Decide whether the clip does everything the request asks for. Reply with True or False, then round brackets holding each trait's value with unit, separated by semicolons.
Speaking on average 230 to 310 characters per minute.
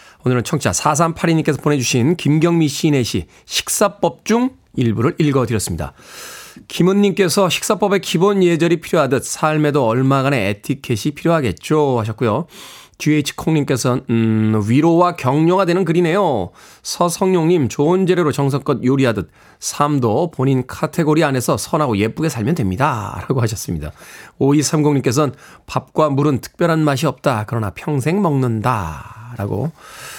False (320 characters per minute)